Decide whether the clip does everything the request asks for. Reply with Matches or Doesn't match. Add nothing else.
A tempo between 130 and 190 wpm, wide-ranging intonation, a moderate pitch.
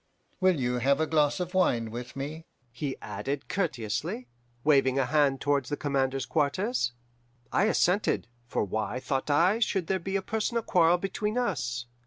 Matches